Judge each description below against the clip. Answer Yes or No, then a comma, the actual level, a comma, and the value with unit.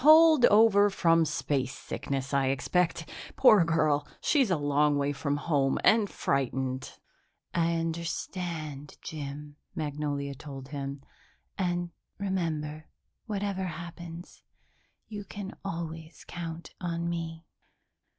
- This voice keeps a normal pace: No, slow, 100 wpm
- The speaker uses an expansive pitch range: No, average, 3.7 semitones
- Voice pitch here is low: No, medium, 165 Hz